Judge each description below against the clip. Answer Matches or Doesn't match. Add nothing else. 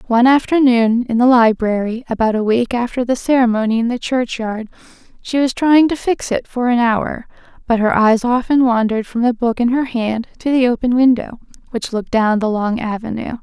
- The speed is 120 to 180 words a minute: Doesn't match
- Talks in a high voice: Matches